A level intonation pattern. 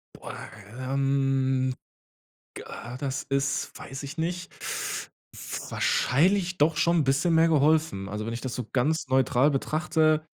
No: average, 3.4 semitones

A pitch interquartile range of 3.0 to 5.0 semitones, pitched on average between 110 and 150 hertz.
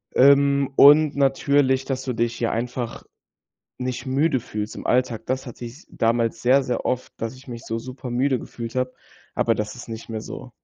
No: narrow, 2.6 semitones; low, 125 Hz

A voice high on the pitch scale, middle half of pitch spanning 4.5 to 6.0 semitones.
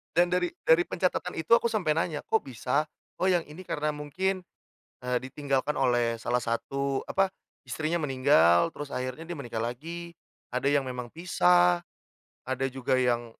No: medium, 140 Hz; average, 5.2 semitones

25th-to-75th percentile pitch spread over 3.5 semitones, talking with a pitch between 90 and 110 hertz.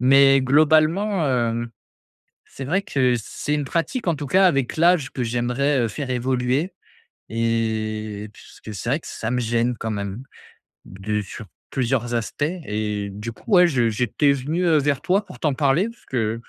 No: average, 4.6 semitones; low, 130 Hz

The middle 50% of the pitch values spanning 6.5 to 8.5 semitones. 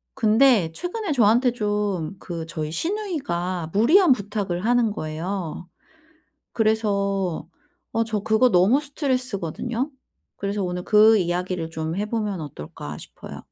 No: average, 5.3 semitones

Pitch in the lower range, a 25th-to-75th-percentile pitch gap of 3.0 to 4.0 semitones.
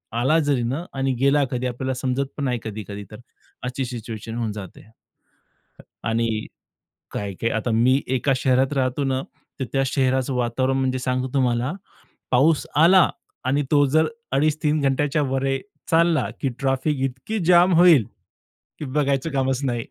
No: low, 130 Hz; narrow, 2.6 semitones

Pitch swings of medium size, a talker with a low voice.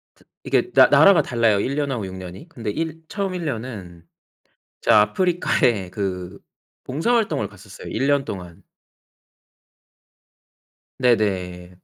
No: wide, 8.1 semitones; low, 110 Hz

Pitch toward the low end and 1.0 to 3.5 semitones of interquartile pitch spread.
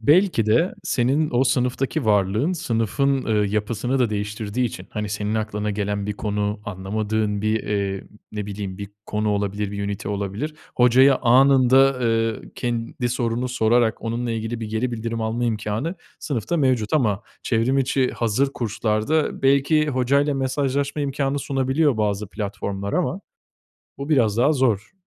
No: low, 115 Hz; average, 4.2 semitones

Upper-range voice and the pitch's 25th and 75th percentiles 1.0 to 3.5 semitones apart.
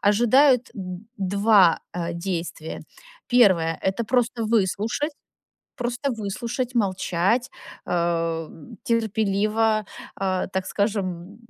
No: high, 205 Hz; average, 4.1 semitones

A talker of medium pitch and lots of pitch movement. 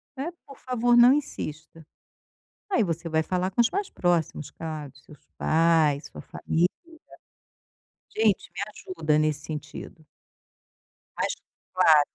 Yes: medium, 165 Hz; wide, 6.1 semitones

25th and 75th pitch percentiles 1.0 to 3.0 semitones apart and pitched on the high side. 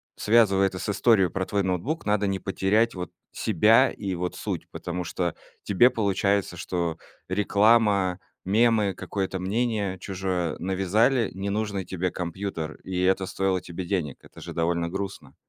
No: narrow, 2.4 semitones; very low, 95 Hz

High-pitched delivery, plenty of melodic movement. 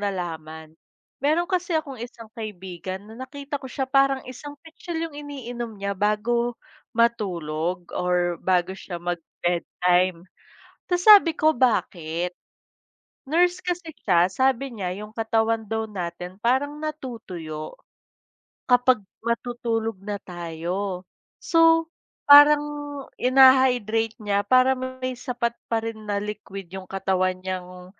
Yes: high, 225 Hz; wide, 6.3 semitones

